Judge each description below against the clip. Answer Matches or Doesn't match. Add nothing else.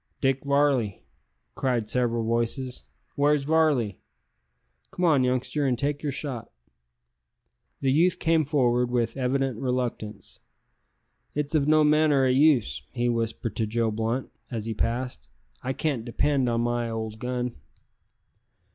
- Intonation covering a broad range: Doesn't match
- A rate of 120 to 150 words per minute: Matches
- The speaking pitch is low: Matches